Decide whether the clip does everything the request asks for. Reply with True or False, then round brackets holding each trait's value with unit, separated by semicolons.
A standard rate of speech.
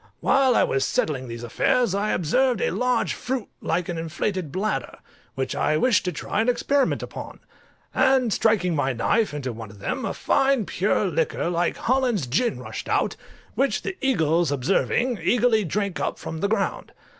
True (175 wpm)